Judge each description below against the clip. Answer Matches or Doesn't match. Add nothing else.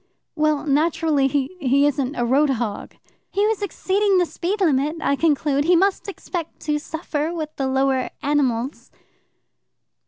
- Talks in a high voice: Matches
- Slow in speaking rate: Doesn't match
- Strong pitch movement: Doesn't match